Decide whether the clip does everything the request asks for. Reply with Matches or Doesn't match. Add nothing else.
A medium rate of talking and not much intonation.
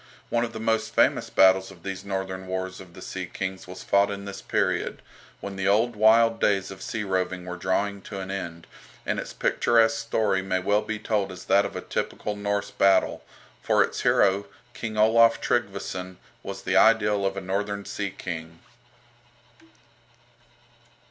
Matches